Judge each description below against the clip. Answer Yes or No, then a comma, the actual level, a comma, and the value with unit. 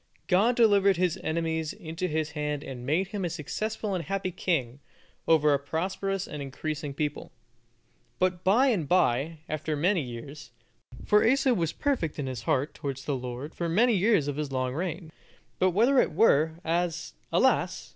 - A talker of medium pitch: Yes, medium, 165 Hz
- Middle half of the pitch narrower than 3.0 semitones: No, average, 4.6 semitones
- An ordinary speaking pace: Yes, average, 170 wpm